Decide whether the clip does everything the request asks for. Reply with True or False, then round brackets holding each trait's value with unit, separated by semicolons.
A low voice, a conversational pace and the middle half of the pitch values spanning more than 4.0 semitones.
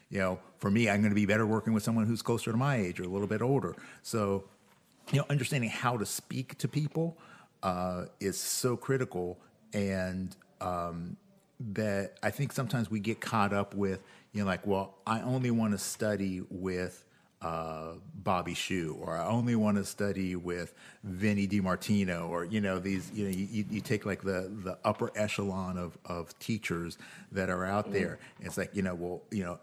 False (100 Hz; 195 wpm; 3.3 semitones)